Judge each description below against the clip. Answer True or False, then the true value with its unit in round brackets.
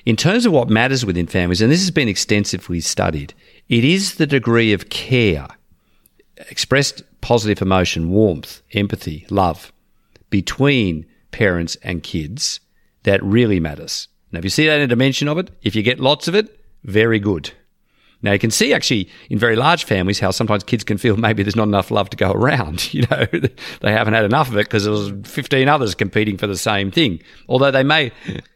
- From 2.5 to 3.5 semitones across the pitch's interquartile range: False (5.0 semitones)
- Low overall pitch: True (105 Hz)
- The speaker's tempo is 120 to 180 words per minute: False (195 wpm)